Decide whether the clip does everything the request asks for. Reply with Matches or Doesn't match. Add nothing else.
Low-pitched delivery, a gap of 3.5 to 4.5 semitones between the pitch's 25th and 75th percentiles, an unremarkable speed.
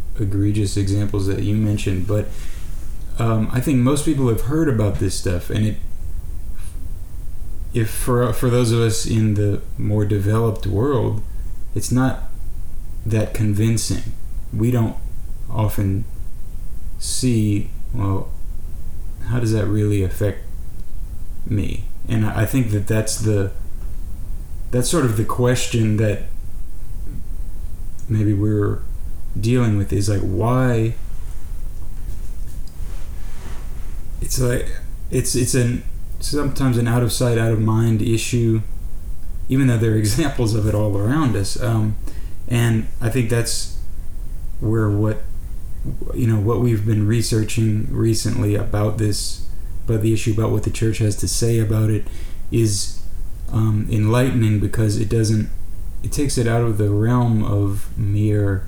Doesn't match